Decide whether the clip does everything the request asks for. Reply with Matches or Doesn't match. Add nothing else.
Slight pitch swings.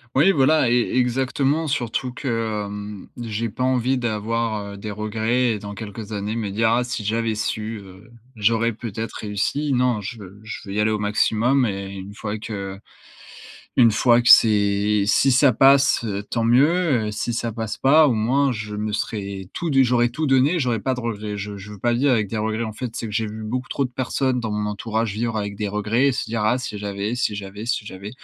Doesn't match